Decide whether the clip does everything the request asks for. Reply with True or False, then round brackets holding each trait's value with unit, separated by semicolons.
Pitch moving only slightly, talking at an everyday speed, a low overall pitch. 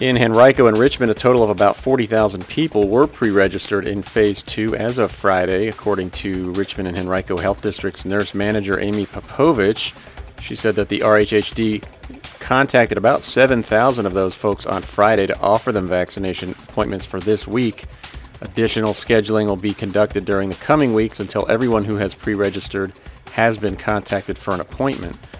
True (2.1 semitones; 165 wpm; 105 Hz)